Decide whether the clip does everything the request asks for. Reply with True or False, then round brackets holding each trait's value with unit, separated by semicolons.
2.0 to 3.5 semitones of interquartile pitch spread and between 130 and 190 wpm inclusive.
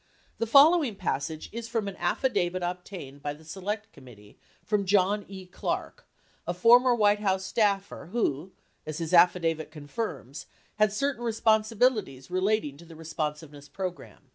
False (5.4 semitones; 150 wpm)